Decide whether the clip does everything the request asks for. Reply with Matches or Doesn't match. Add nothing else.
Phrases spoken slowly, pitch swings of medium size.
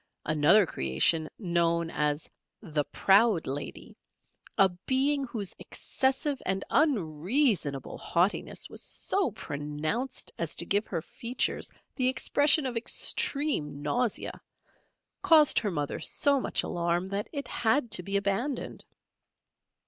Doesn't match